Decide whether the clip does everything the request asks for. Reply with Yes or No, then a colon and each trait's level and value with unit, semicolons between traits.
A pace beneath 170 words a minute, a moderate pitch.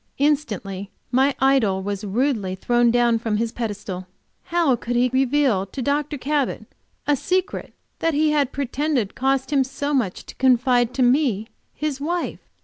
No: average, 155 wpm; very high, 255 Hz